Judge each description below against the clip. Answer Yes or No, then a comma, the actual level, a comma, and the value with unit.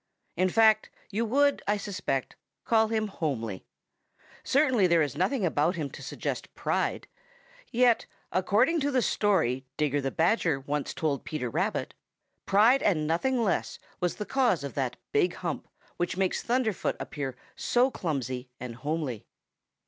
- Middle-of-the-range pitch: Yes, medium, 180 Hz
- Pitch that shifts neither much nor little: No, wide, 7.7 semitones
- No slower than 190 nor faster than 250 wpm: No, average, 150 wpm